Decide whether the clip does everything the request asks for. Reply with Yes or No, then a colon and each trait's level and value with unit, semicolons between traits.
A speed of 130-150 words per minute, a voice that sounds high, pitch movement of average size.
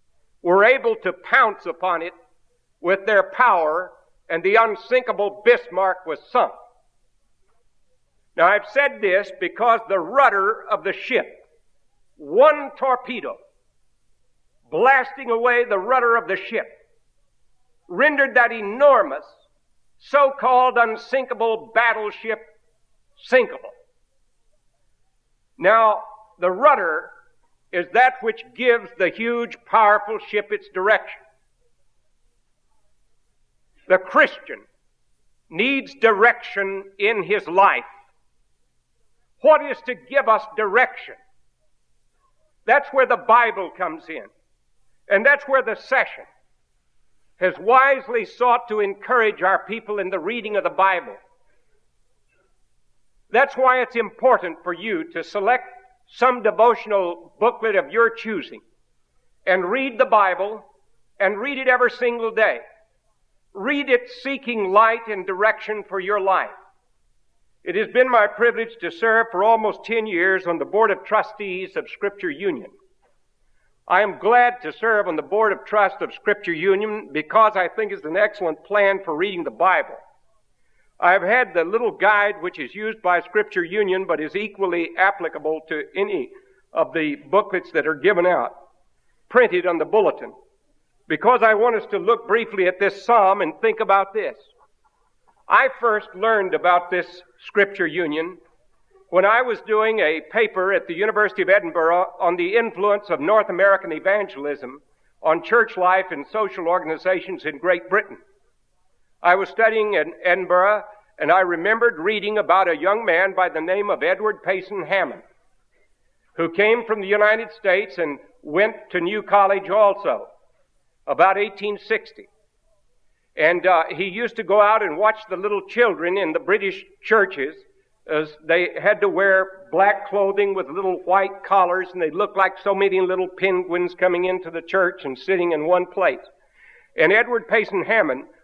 Yes: average, 140 wpm; high, 210 Hz; average, 4.3 semitones